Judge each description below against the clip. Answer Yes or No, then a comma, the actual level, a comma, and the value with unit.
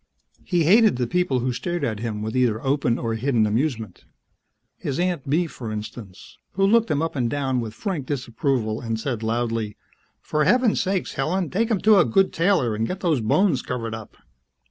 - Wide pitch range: Yes, wide, 7.6 semitones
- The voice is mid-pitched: No, low, 130 Hz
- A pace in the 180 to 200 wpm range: Yes, average, 190 wpm